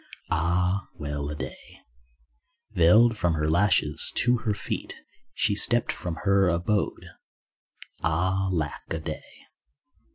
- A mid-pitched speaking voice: No, very low, 90 Hz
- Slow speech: Yes, slow, 120 wpm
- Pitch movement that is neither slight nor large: Yes, average, 4.2 semitones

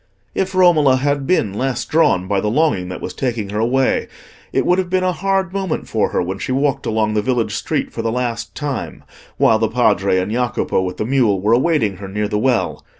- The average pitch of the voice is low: Yes, low, 125 Hz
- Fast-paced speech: Yes, fast, 220 wpm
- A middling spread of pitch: No, wide, 6.2 semitones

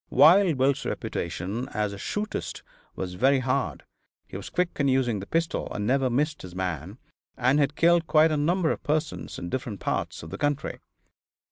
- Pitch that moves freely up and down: Yes, wide, 7.0 semitones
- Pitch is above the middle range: No, low, 135 Hz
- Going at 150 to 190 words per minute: Yes, average, 180 wpm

